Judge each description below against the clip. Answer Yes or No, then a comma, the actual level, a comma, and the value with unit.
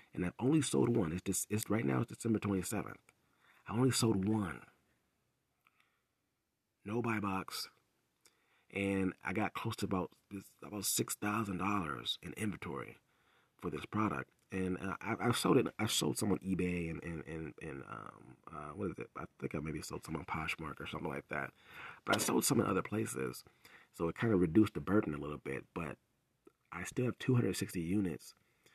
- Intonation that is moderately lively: Yes, average, 3.4 semitones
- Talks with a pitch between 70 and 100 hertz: Yes, very low, 95 Hz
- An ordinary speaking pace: Yes, average, 195 wpm